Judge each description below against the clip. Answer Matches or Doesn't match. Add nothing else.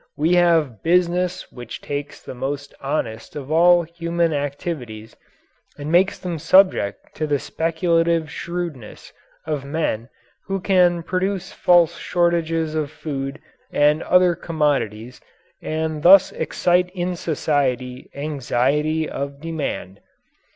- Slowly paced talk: Matches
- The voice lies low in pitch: Doesn't match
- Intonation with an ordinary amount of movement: Matches